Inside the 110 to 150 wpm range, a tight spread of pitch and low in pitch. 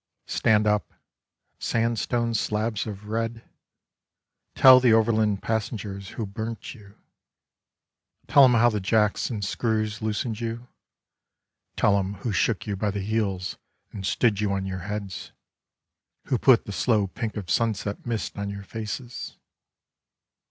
Yes: average, 140 wpm; narrow, 2.2 semitones; low, 110 Hz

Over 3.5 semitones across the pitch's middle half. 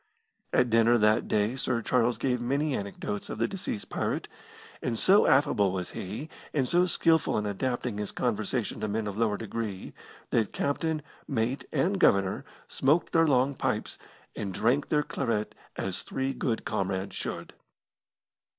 Yes: average, 4.7 semitones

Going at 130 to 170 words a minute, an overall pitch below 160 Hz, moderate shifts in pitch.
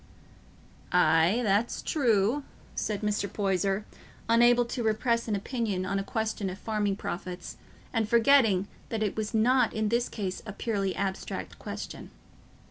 No: average, 140 wpm; high, 215 Hz; average, 3.0 semitones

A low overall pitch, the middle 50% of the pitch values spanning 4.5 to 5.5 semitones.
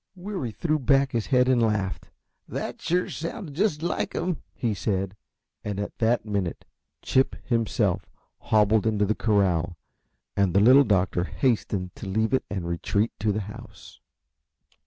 Yes: low, 110 Hz; average, 5.0 semitones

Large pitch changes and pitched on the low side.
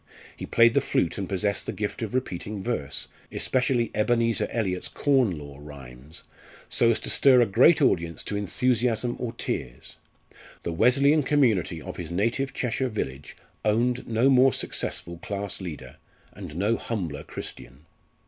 Yes: wide, 6.2 semitones; low, 110 Hz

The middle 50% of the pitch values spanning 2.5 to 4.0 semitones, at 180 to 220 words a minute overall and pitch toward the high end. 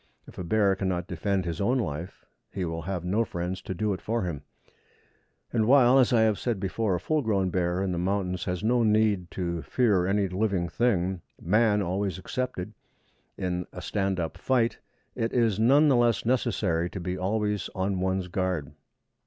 No: average, 3.6 semitones; average, 185 wpm; very low, 95 Hz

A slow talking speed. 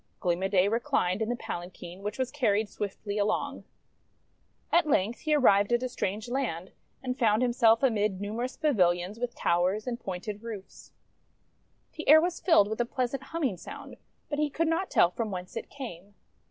No: average, 180 wpm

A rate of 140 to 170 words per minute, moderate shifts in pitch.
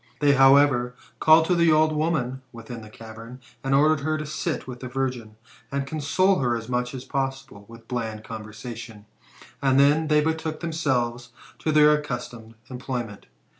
Yes: average, 165 wpm; average, 4.2 semitones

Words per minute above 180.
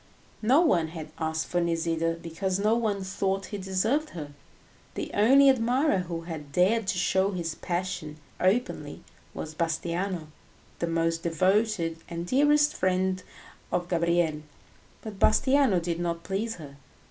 No: average, 140 wpm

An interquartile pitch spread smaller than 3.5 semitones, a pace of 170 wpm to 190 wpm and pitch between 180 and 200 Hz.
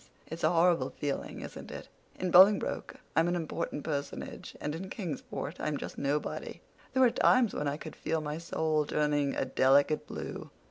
No: average, 3.0 semitones; average, 175 wpm; medium, 155 Hz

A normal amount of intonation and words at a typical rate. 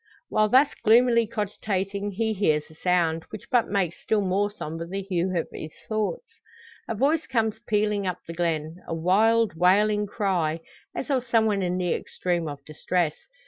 Yes: average, 4.1 semitones; average, 175 wpm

